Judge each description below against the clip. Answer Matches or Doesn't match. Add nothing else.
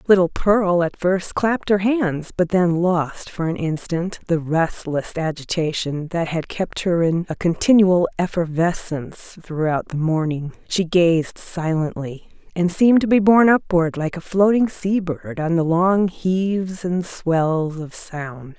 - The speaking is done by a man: Doesn't match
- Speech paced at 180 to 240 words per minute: Doesn't match